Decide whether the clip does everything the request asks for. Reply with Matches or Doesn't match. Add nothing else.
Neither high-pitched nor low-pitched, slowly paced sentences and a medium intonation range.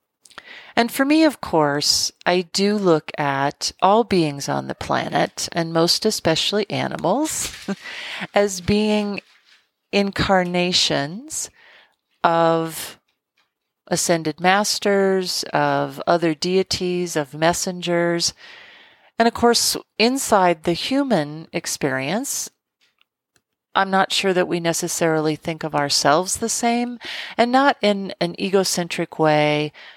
Matches